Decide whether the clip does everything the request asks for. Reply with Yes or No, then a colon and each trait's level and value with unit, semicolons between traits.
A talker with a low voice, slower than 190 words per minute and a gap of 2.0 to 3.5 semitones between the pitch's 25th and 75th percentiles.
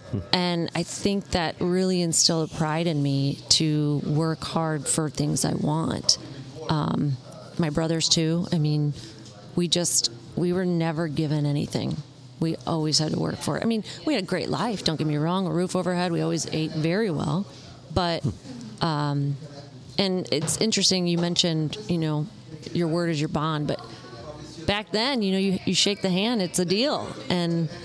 No: medium, 160 Hz; average, 180 wpm; average, 3.2 semitones